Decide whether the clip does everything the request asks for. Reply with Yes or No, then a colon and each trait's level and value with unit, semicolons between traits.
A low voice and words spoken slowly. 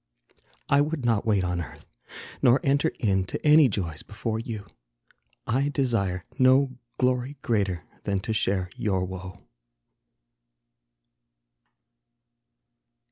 Yes: low, 110 Hz; slow, 110 wpm